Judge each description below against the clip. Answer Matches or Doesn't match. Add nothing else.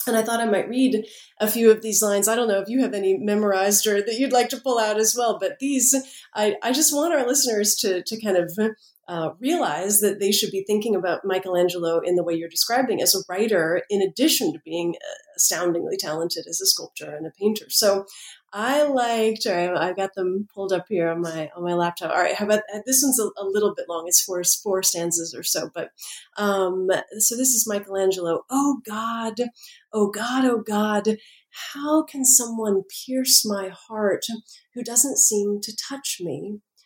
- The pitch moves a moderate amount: Matches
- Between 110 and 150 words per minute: Doesn't match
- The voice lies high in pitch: Matches